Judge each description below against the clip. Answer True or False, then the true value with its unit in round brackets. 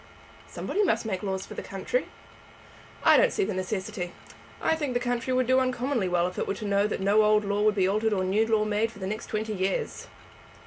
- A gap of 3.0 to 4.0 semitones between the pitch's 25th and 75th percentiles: True (3.6 semitones)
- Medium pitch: False (215 Hz)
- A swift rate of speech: True (230 wpm)